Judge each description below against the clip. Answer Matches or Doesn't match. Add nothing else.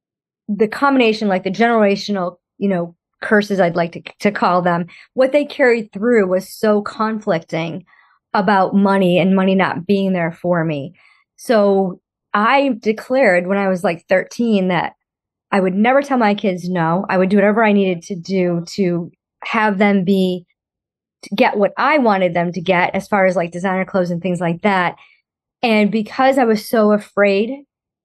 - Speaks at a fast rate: Doesn't match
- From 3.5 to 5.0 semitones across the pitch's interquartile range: Doesn't match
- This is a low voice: Doesn't match